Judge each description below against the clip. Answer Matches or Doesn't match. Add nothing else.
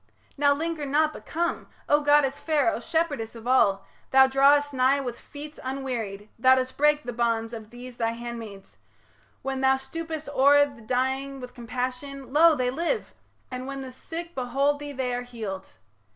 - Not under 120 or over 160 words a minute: Doesn't match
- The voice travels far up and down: Doesn't match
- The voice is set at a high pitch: Matches